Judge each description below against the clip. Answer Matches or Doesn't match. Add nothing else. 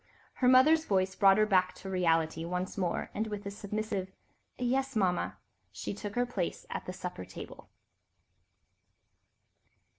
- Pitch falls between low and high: Doesn't match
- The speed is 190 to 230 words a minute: Doesn't match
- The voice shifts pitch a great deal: Doesn't match